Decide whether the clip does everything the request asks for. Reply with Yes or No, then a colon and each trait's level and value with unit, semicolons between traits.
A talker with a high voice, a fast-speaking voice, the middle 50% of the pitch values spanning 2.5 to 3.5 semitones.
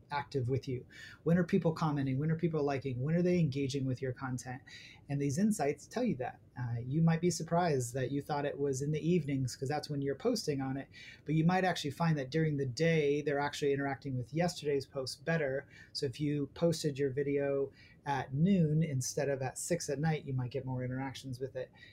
No: medium, 140 Hz; fast, 220 wpm; average, 3.0 semitones